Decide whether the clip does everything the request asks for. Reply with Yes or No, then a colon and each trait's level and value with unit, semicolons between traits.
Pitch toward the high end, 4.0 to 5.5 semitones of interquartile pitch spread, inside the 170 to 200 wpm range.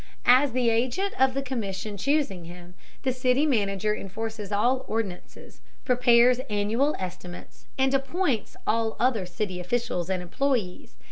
No: high, 225 Hz; average, 4.9 semitones; slow, 135 wpm